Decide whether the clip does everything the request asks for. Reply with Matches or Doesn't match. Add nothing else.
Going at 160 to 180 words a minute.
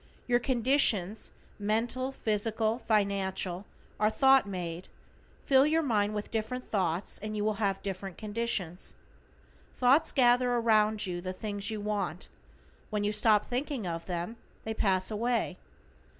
Doesn't match